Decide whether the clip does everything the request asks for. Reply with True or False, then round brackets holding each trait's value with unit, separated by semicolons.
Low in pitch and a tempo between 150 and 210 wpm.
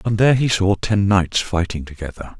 True (100 Hz; 200 wpm)